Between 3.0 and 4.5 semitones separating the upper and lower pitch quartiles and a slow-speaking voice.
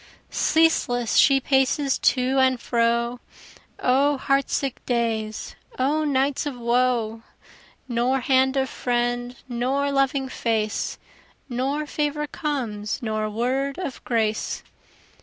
No: narrow, 2.6 semitones; slow, 110 wpm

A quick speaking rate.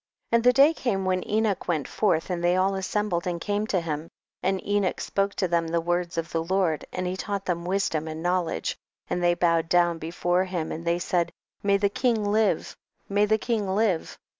Yes: fast, 215 wpm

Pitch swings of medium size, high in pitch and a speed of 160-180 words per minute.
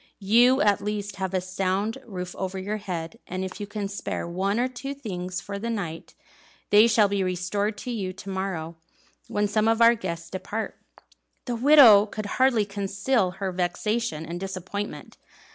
Yes: average, 3.0 semitones; high, 200 Hz; average, 175 wpm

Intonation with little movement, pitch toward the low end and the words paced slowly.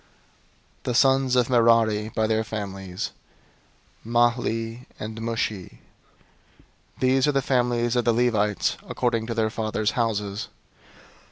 Yes: narrow, 2.0 semitones; low, 115 Hz; slow, 120 wpm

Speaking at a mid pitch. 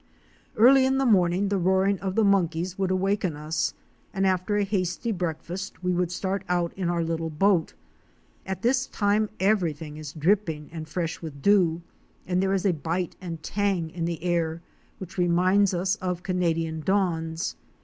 Yes: medium, 180 Hz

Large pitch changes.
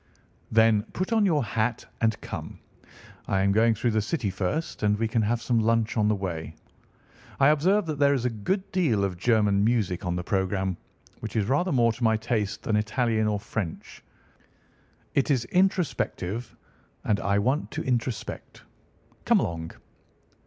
No: average, 4.2 semitones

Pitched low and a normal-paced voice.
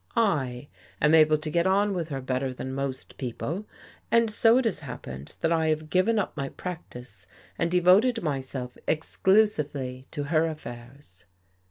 No: medium, 155 Hz; average, 160 wpm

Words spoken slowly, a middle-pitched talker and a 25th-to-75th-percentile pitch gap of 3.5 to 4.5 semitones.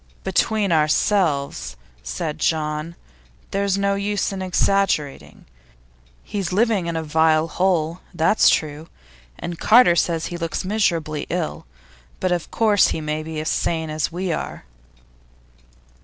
Yes: slow, 130 wpm; medium, 170 Hz; average, 3.8 semitones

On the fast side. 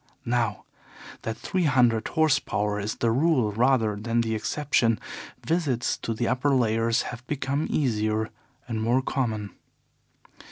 No: slow, 135 wpm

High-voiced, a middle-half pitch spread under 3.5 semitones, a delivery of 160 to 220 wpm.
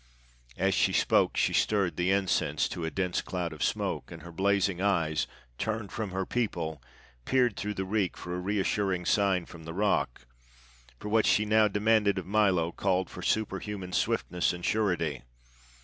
No: very low, 95 Hz; average, 3.0 semitones; average, 170 wpm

